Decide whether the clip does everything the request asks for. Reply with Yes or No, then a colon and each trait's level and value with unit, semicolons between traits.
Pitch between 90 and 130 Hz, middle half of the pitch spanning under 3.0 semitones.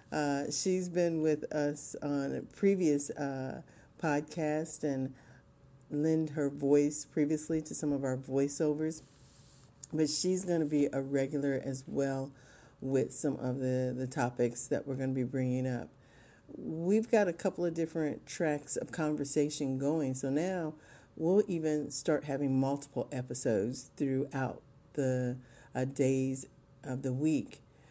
No: medium, 140 Hz; narrow, 2.6 semitones